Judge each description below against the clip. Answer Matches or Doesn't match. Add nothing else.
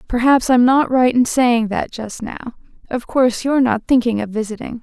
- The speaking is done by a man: Doesn't match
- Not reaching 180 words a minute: Doesn't match